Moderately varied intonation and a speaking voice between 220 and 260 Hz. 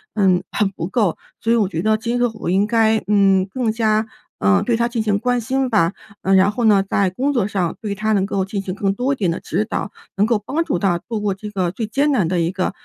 No: average, 3.2 semitones; high, 210 Hz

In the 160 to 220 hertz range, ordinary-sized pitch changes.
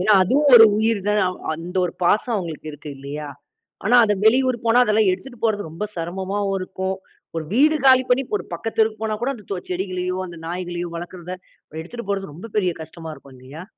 Yes: high, 190 Hz; average, 4.4 semitones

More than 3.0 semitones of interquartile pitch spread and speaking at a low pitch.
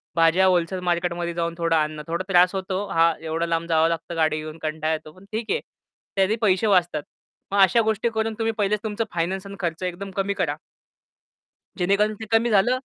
No: average, 3.4 semitones; medium, 180 Hz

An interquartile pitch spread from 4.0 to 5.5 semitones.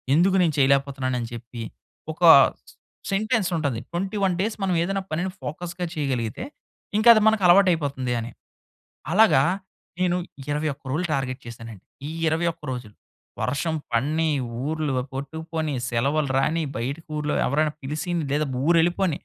Yes: average, 4.6 semitones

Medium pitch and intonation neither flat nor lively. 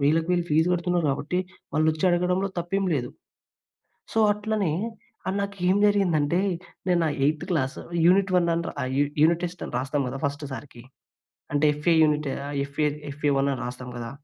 Yes: medium, 160 Hz; average, 3.8 semitones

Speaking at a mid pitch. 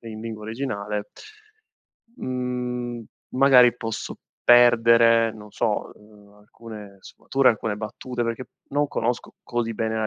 No: low, 115 Hz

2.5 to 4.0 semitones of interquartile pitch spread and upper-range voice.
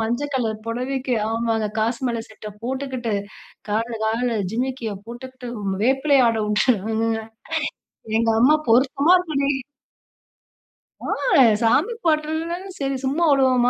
Yes: average, 3.4 semitones; very high, 250 Hz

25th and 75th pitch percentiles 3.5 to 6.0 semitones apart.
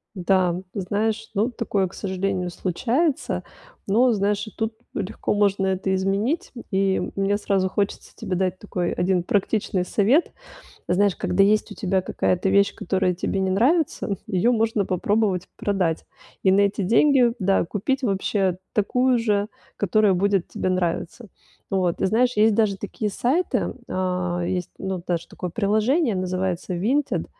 No: average, 2.9 semitones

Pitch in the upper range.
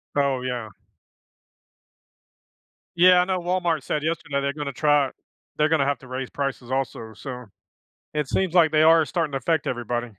No: medium, 145 Hz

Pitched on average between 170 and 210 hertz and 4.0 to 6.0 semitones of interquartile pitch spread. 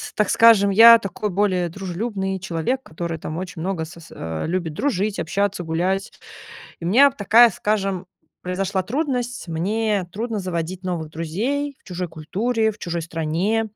Yes: high, 190 Hz; average, 4.3 semitones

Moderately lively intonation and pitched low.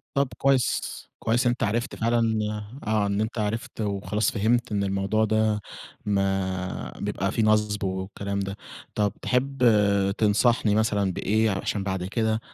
No: narrow, 2.2 semitones; low, 105 Hz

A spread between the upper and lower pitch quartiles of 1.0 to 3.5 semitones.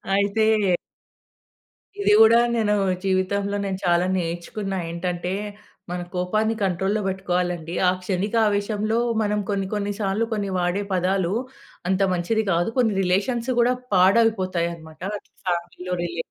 Yes: average, 2.7 semitones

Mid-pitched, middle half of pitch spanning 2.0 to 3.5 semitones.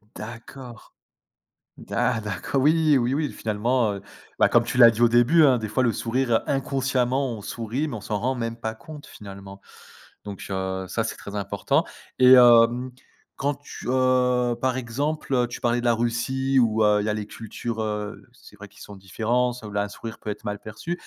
No: low, 120 Hz; average, 3.2 semitones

